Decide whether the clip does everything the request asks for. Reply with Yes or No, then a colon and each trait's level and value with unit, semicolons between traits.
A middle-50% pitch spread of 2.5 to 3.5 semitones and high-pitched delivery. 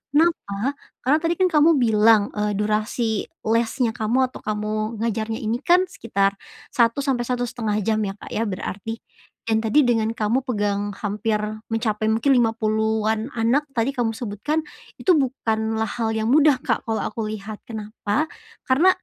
Yes: average, 3.1 semitones; high, 225 Hz